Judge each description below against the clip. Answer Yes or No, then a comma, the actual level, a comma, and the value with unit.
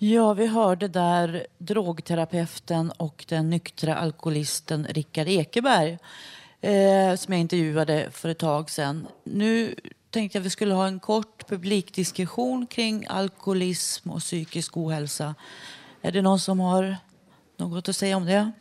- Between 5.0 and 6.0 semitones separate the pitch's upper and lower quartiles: No, average, 3.7 semitones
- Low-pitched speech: No, medium, 180 Hz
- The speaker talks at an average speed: Yes, average, 140 wpm